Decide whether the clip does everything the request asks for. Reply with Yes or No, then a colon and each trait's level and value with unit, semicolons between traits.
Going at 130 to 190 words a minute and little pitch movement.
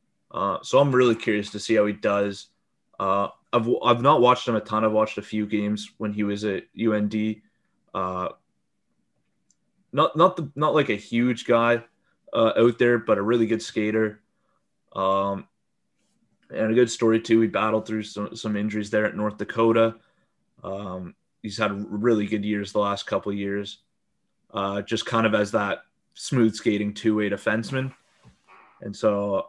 Yes: average, 175 wpm; narrow, 1.7 semitones